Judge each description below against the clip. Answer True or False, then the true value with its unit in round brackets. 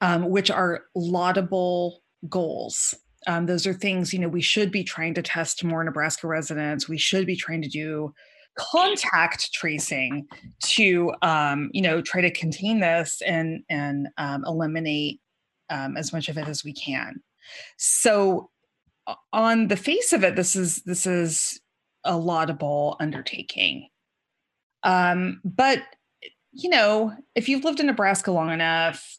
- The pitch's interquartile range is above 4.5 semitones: False (3.4 semitones)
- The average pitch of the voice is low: False (175 Hz)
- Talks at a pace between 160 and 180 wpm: False (150 wpm)